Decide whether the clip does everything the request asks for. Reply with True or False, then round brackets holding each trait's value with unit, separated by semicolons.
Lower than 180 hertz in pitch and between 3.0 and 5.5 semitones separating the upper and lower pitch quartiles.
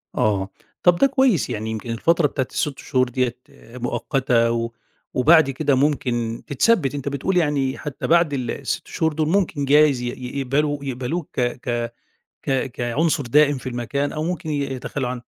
True (135 Hz; 3.7 semitones)